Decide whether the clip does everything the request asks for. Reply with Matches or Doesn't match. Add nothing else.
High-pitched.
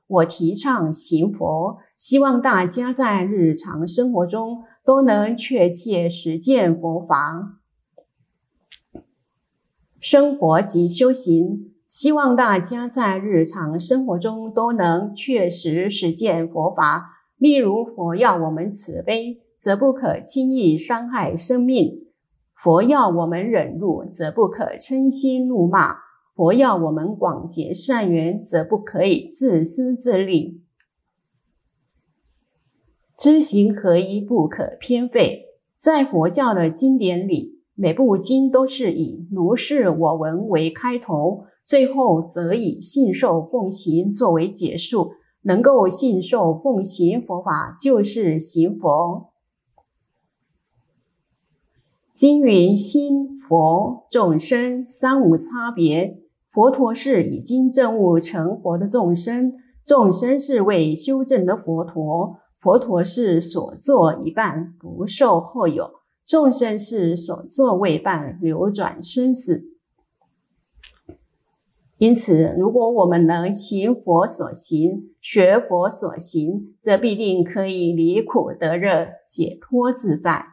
Matches